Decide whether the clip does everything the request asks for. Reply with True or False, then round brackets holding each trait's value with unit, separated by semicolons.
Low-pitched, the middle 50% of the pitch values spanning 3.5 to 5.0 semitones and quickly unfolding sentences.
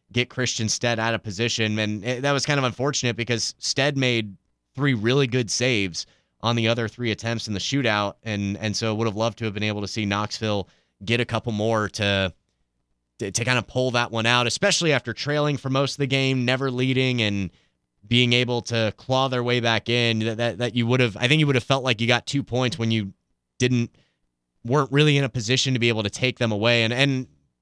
False (120 Hz; 2.9 semitones; 230 wpm)